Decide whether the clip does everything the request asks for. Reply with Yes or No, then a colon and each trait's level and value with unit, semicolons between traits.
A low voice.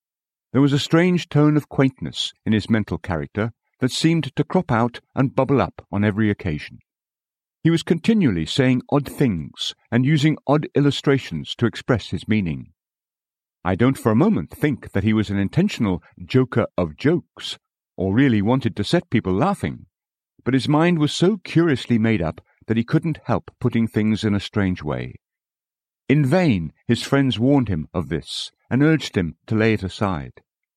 Yes: low, 120 Hz